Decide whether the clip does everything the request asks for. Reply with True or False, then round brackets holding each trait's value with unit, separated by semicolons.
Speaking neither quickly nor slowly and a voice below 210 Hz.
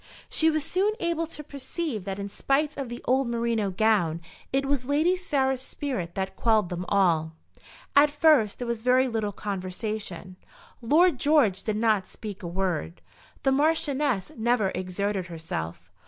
False (155 wpm; 230 Hz)